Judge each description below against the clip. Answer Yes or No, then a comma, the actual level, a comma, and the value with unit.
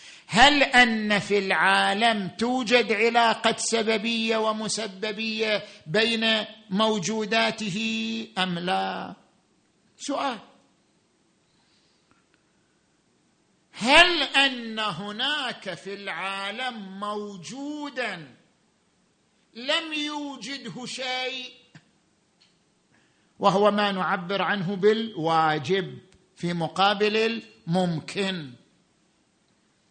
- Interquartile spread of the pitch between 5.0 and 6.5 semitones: No, average, 3.2 semitones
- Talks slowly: Yes, slow, 60 wpm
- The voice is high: Yes, high, 215 Hz